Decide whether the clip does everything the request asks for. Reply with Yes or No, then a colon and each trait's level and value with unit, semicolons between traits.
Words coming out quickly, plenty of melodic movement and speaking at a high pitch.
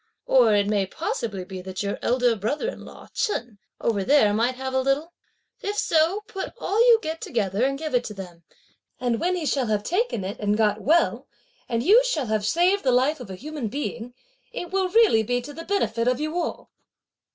Yes: fast, 210 wpm; wide, 7.5 semitones; very high, 255 Hz